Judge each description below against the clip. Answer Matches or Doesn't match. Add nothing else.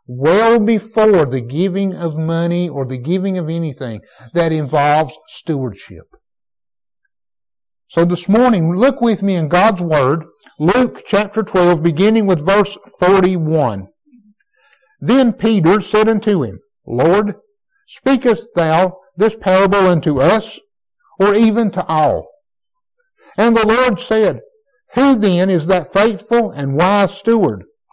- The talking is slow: Matches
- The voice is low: Doesn't match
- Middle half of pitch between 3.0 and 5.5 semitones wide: Matches